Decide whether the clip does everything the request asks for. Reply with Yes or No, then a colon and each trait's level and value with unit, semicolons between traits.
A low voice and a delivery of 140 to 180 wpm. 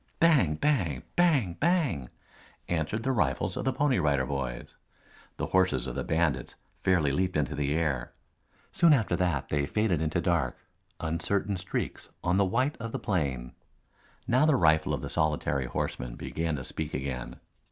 Yes: very low, 85 Hz; average, 165 wpm